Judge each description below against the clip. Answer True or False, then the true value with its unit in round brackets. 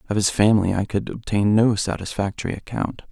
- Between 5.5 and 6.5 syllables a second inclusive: True (5.8 syllables/s)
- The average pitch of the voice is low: True (105 Hz)